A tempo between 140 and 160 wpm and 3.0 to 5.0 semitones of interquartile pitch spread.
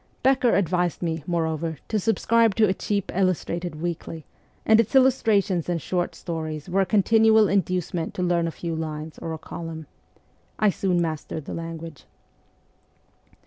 Yes: average, 150 wpm; average, 3.6 semitones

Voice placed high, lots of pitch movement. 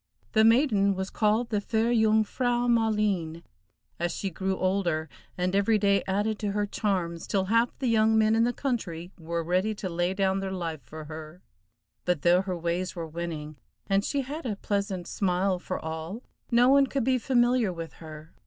No: high, 195 Hz; average, 4.3 semitones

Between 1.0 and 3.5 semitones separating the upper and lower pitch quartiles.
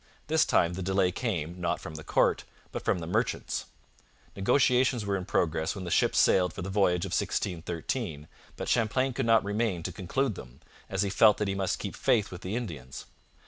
No: average, 4.6 semitones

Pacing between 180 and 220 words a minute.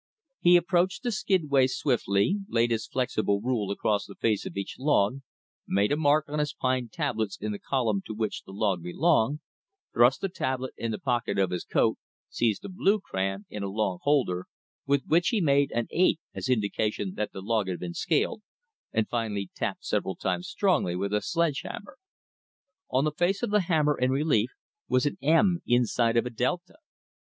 Yes: average, 190 wpm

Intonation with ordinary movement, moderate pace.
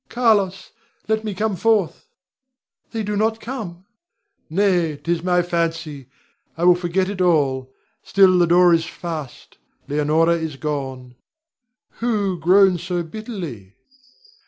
No: average, 3.9 semitones; slow, 125 wpm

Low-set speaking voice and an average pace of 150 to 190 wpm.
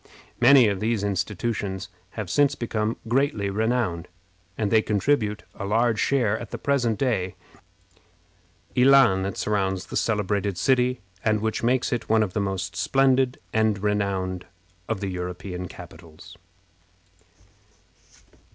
No: low, 105 Hz; slow, 135 wpm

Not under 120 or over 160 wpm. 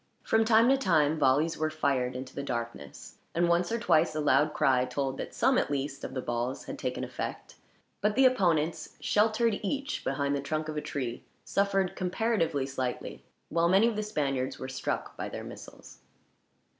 No: average, 185 wpm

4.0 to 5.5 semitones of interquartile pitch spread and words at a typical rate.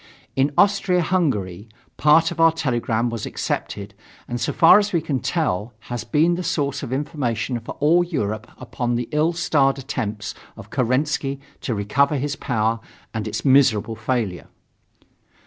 Yes: average, 5.2 semitones; average, 155 wpm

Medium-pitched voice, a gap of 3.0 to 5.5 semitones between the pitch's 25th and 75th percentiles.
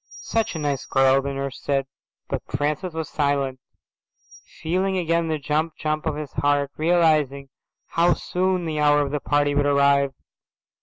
No: medium, 150 Hz; narrow, 2.5 semitones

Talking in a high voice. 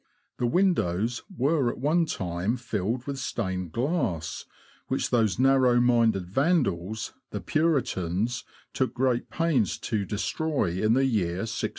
No: low, 120 Hz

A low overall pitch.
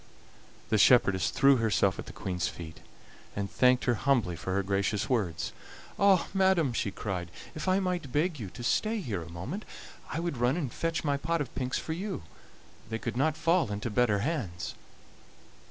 Yes: low, 125 Hz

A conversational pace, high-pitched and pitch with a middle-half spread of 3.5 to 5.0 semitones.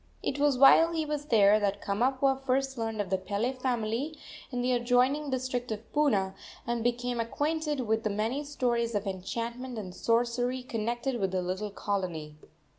Yes: average, 170 wpm; high, 240 Hz; average, 3.8 semitones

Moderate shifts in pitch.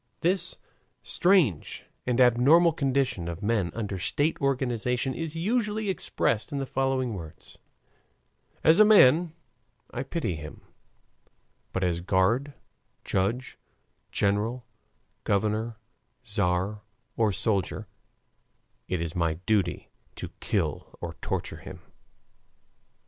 No: wide, 6.7 semitones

